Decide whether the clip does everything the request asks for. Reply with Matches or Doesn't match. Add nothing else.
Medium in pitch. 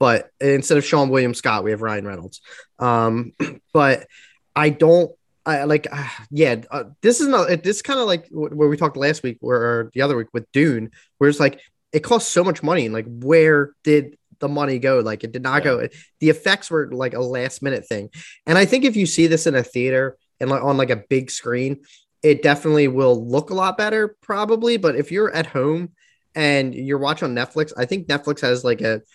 Matches